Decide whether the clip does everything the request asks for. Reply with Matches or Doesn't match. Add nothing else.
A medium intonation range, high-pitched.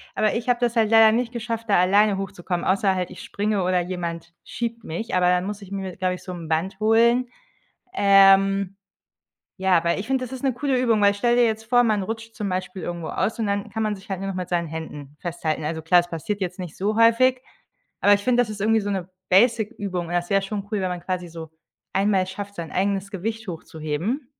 Matches